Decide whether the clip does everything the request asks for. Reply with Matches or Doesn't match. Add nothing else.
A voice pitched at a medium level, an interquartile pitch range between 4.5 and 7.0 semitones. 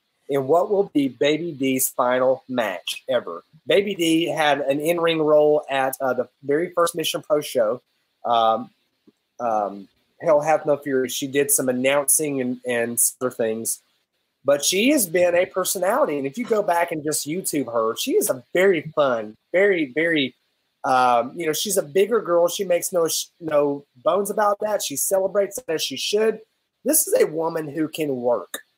Matches